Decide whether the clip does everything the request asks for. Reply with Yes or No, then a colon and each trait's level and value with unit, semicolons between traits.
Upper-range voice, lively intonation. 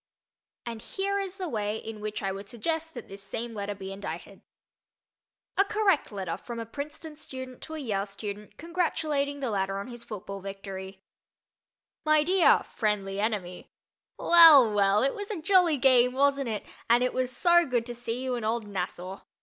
Yes: high, 235 Hz; wide, 6.9 semitones